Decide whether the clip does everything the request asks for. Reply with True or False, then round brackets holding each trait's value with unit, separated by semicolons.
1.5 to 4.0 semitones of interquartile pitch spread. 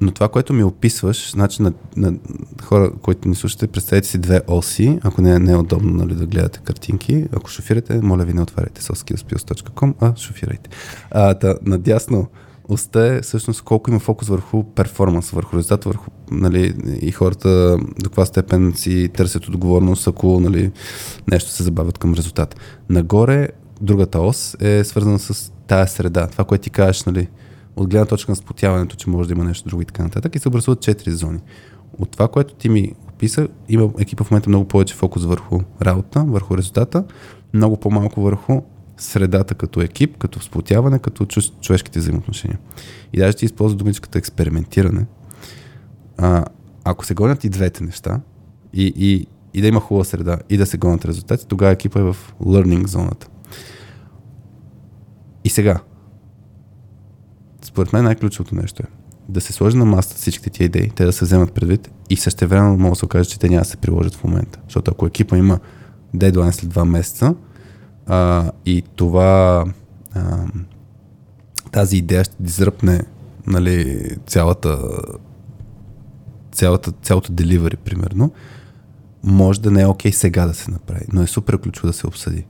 True (3.4 semitones)